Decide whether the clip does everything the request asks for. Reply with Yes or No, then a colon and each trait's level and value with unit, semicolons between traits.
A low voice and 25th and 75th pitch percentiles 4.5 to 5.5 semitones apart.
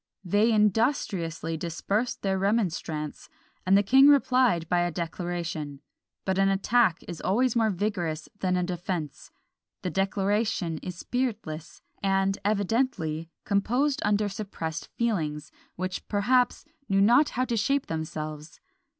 No: high, 195 Hz; average, 4.8 semitones